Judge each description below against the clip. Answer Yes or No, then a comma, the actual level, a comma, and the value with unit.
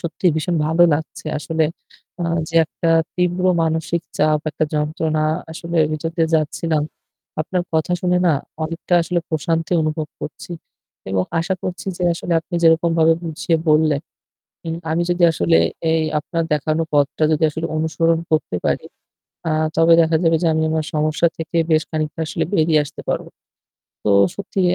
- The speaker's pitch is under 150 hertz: No, medium, 160 Hz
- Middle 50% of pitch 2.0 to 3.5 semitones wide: No, narrow, 1.4 semitones